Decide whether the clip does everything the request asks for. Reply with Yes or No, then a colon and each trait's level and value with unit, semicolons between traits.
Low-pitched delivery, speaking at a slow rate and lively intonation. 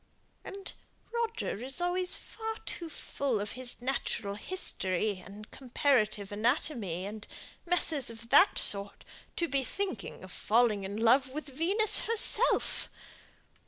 No: very high, 255 Hz; slow, 125 wpm; wide, 8.6 semitones